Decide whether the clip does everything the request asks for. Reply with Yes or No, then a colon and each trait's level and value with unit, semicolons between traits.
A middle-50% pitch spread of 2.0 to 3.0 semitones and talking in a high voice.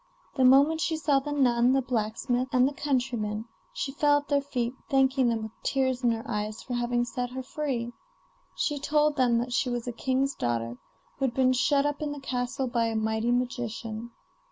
Yes: narrow, 2.6 semitones; very high, 250 Hz